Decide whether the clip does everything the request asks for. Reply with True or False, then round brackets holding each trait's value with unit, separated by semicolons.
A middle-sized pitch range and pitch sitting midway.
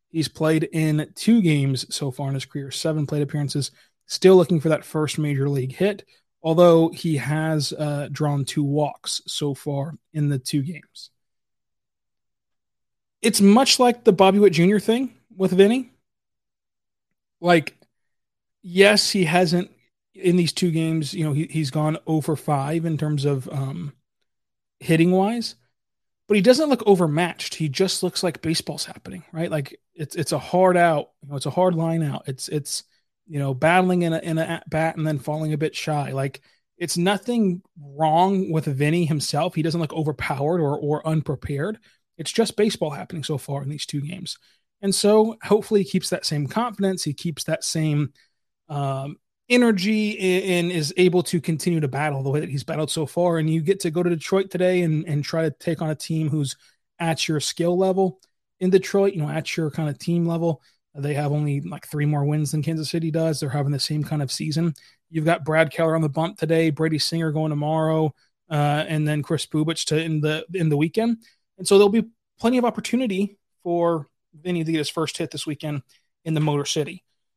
True (3.4 semitones; 160 Hz)